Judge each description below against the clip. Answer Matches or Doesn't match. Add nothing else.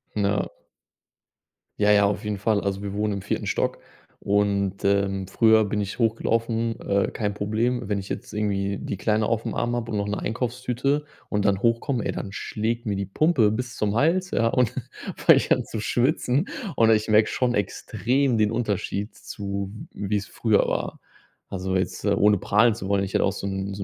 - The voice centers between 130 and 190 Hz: Doesn't match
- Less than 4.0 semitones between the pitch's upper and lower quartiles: Matches